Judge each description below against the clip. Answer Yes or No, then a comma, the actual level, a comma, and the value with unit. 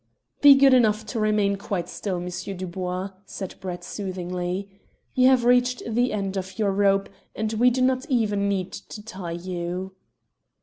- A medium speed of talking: Yes, average, 165 wpm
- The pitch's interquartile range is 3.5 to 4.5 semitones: Yes, average, 3.8 semitones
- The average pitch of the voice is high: Yes, high, 200 Hz